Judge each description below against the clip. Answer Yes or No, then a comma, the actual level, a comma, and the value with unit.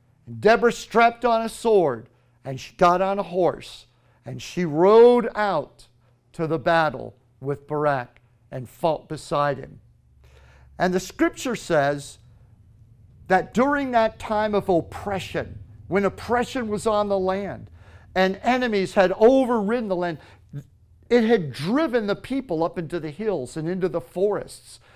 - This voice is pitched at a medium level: Yes, medium, 170 Hz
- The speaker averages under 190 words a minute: Yes, average, 140 wpm